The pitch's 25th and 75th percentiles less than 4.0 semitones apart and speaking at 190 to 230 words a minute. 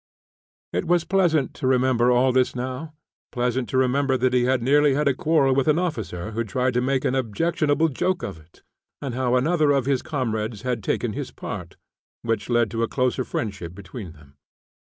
Yes: average, 3.4 semitones; average, 195 wpm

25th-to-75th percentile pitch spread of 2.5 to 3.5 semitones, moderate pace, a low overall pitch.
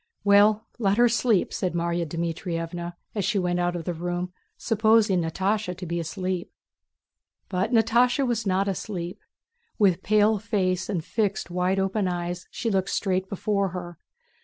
No: average, 3.1 semitones; average, 155 wpm; high, 190 Hz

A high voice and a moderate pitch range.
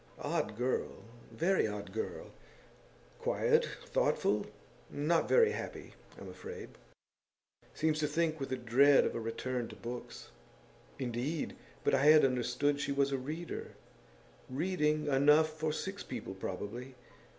No: medium, 140 Hz; average, 4.2 semitones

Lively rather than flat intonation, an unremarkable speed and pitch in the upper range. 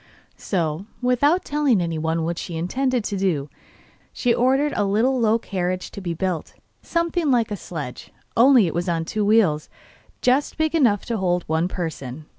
Yes: wide, 7.0 semitones; average, 170 wpm; high, 200 Hz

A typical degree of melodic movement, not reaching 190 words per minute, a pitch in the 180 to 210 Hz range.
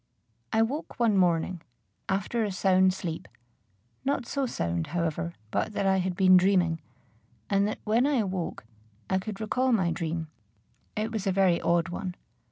Yes: average, 3.9 semitones; average, 165 wpm; high, 190 Hz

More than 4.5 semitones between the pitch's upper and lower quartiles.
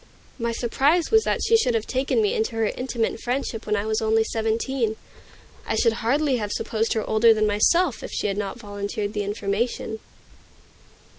No: average, 3.3 semitones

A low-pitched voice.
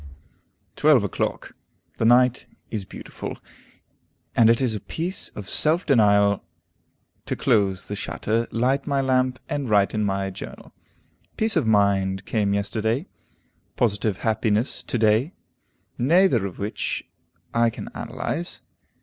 Yes: low, 110 Hz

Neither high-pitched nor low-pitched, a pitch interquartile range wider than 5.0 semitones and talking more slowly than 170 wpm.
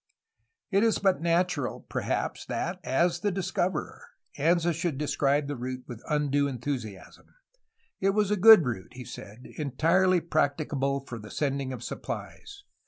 Yes: medium, 150 Hz; wide, 5.4 semitones; average, 150 wpm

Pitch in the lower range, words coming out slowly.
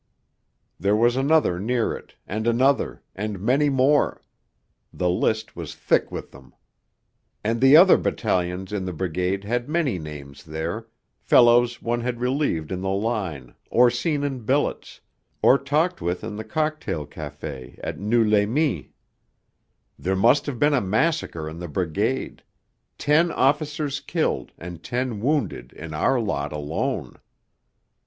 No: low, 115 Hz; average, 145 wpm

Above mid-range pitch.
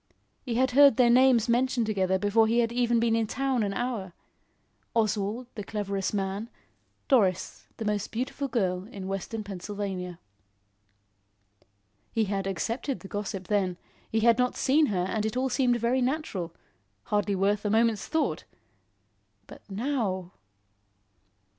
Yes: high, 220 Hz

